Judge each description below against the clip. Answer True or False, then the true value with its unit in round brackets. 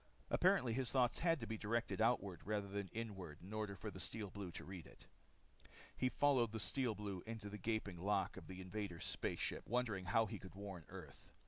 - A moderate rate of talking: False (210 wpm)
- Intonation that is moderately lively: True (3.1 semitones)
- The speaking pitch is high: False (105 Hz)